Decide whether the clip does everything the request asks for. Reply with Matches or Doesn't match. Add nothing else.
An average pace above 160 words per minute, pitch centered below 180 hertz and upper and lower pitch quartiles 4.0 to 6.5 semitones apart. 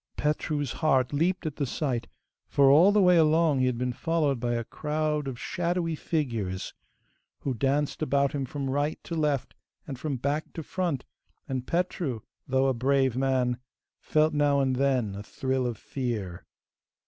Doesn't match